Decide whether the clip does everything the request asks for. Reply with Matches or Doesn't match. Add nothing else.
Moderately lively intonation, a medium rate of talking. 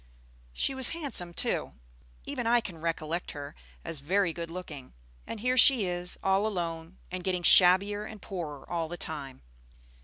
Matches